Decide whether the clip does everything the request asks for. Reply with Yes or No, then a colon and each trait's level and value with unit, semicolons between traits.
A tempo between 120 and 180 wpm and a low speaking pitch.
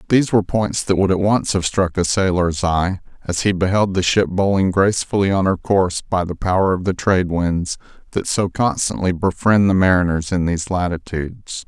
No: average, 195 wpm; very low, 95 Hz